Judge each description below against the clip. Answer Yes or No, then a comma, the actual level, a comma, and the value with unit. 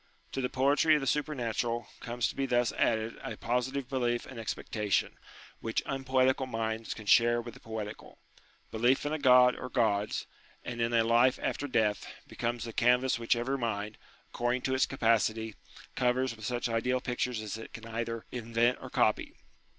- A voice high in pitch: No, low, 120 Hz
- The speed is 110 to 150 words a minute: No, average, 180 wpm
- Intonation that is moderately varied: No, narrow, 2.1 semitones